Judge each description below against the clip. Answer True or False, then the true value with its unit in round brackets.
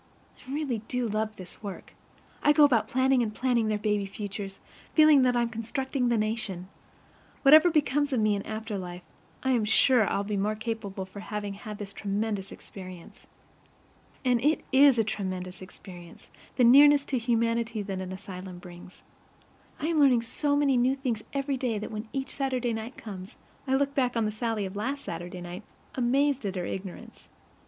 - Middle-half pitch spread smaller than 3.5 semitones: False (4.7 semitones)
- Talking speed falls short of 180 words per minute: False (185 wpm)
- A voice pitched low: False (225 Hz)